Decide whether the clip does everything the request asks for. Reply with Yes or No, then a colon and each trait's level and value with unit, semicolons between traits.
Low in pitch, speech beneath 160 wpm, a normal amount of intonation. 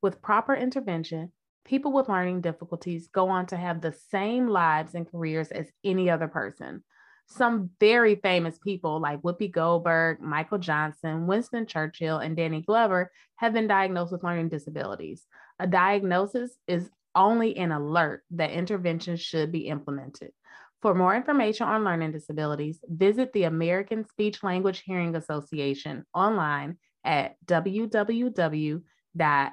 No: medium, 175 Hz; slow, 135 wpm; average, 4.3 semitones